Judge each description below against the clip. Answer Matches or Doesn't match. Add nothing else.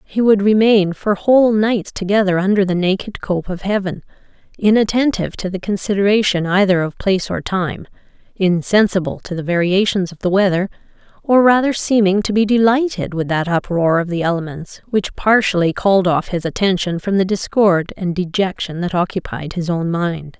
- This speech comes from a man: Doesn't match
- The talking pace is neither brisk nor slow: Matches